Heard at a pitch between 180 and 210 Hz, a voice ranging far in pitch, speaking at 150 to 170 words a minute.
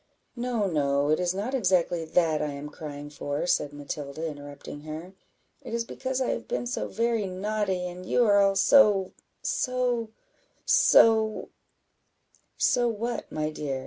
Yes: medium, 185 Hz; wide, 7.2 semitones; average, 155 wpm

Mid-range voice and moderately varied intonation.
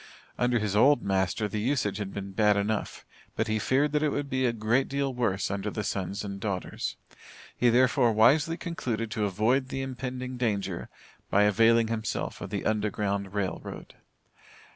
No: low, 110 Hz; average, 4.0 semitones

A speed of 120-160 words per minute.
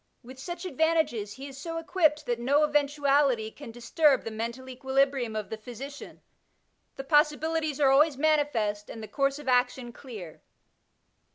Yes: average, 155 wpm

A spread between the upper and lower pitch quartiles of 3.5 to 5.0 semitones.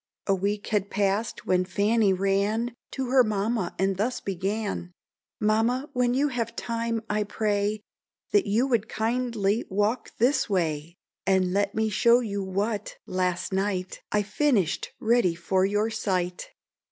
No: average, 3.1 semitones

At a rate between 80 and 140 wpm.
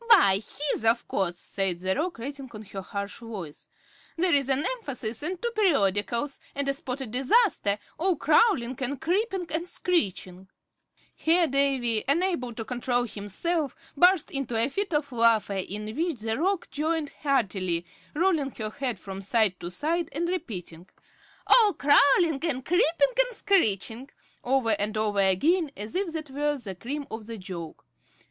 No: average, 160 wpm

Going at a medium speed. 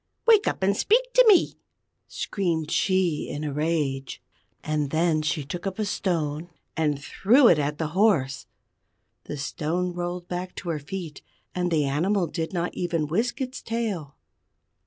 Yes: average, 160 wpm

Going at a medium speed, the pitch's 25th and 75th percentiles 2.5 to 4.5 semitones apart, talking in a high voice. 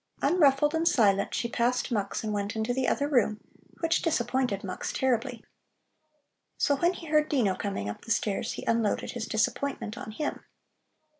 No: average, 165 wpm; average, 4.9 semitones; high, 240 Hz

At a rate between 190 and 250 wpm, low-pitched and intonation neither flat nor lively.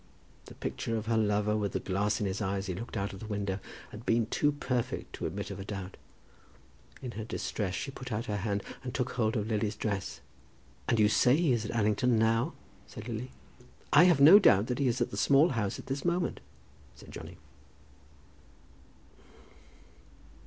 Yes: average, 195 wpm; low, 110 Hz; average, 3.6 semitones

